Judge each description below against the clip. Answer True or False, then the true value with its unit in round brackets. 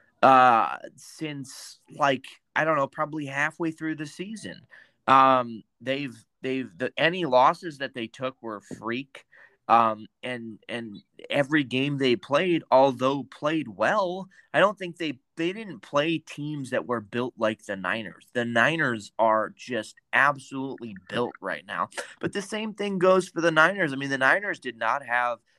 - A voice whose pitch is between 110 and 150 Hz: True (135 Hz)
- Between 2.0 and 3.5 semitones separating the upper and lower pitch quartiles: False (5.1 semitones)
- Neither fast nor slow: True (160 wpm)